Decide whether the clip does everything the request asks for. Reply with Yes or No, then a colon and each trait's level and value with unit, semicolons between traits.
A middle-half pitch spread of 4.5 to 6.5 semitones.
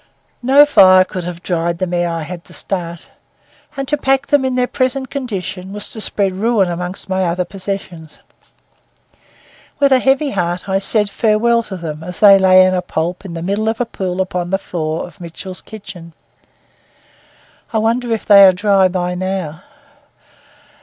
No: average, 3.8 semitones